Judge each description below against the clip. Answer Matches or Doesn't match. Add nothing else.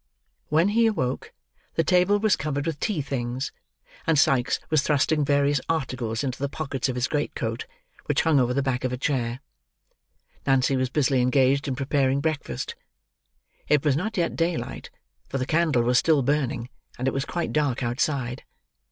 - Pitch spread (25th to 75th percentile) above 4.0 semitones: Doesn't match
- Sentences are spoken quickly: Doesn't match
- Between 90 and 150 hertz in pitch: Matches